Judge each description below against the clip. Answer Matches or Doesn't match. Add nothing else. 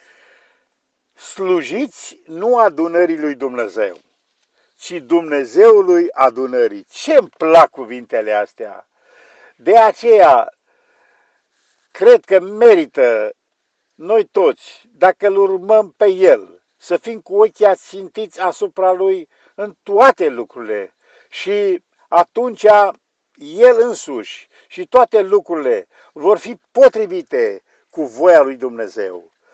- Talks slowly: Matches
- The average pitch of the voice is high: Matches